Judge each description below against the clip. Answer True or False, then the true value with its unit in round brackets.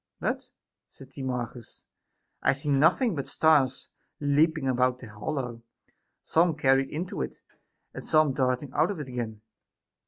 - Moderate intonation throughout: True (3.3 semitones)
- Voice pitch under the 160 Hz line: True (135 Hz)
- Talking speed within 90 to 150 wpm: True (145 wpm)